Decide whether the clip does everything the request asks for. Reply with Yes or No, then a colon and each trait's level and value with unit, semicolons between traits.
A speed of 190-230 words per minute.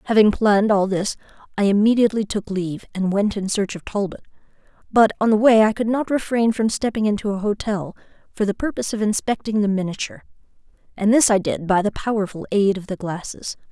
Yes: average, 195 wpm